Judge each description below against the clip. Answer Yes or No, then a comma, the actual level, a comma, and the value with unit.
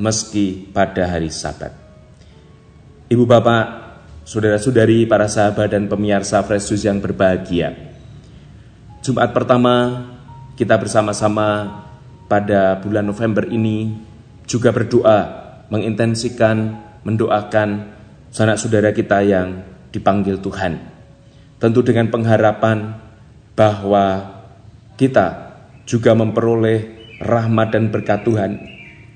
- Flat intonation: Yes, narrow, 2.1 semitones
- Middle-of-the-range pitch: No, low, 110 Hz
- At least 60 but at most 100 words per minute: Yes, average, 90 wpm